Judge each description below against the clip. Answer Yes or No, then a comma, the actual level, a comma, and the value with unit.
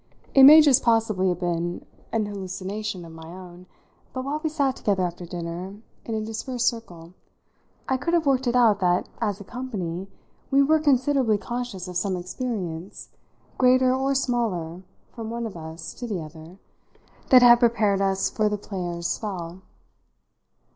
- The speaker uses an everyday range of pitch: No, wide, 5.8 semitones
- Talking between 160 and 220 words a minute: Yes, average, 165 wpm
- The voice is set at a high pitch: Yes, high, 210 Hz